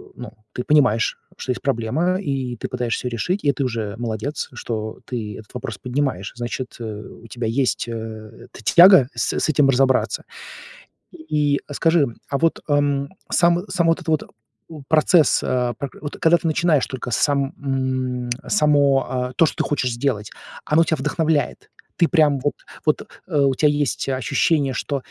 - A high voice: No, medium, 140 Hz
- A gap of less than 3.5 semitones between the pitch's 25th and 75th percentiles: No, average, 3.8 semitones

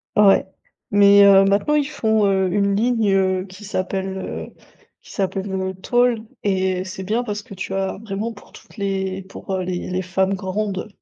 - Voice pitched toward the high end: Yes, high, 195 Hz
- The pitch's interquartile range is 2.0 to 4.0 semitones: No, narrow, 1.6 semitones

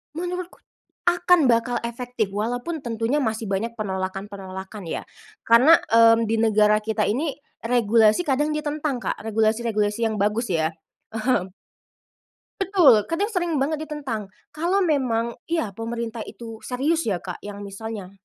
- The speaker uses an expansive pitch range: Yes, wide, 5.7 semitones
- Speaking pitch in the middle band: No, high, 230 Hz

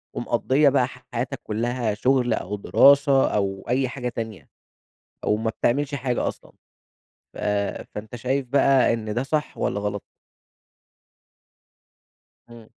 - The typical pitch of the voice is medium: No, low, 120 Hz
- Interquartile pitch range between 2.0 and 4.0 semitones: Yes, average, 3.6 semitones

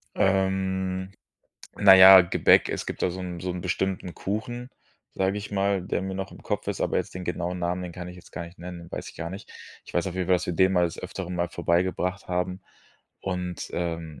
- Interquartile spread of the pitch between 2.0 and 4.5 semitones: No, narrow, 1.5 semitones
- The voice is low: Yes, very low, 90 Hz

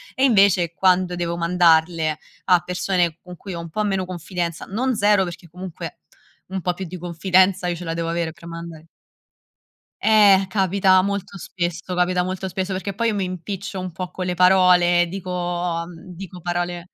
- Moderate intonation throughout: No, narrow, 1.8 semitones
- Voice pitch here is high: No, medium, 180 Hz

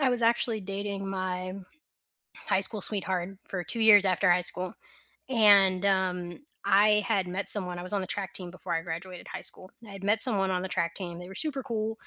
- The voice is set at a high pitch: Yes, high, 195 Hz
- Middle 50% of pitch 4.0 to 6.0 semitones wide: No, narrow, 2.5 semitones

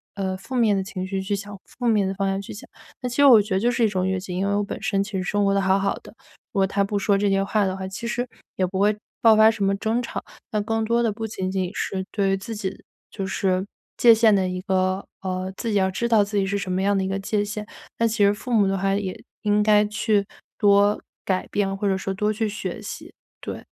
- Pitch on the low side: No, high, 200 Hz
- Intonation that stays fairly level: Yes, narrow, 1.9 semitones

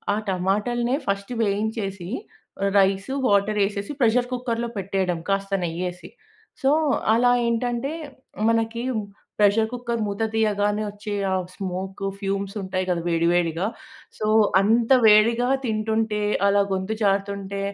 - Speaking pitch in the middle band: No, high, 205 Hz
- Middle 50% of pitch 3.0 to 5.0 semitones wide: No, narrow, 2.6 semitones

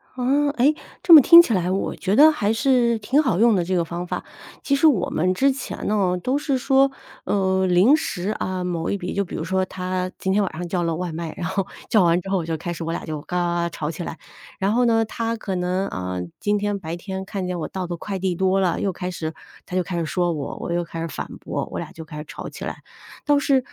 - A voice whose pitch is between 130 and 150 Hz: No, medium, 185 Hz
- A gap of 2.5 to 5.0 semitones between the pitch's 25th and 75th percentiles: Yes, average, 4.5 semitones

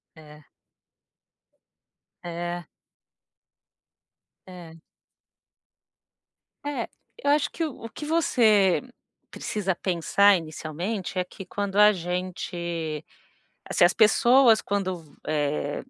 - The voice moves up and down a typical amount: Yes, average, 4.0 semitones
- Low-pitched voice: No, medium, 185 Hz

